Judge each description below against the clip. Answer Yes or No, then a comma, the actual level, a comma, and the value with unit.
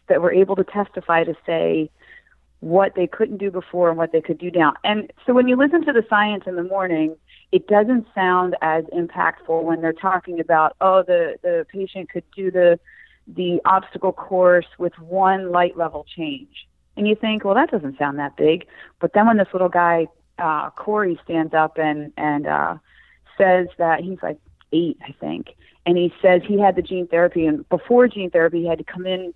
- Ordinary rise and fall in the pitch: Yes, average, 3.4 semitones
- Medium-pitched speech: Yes, medium, 180 Hz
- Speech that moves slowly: No, average, 200 wpm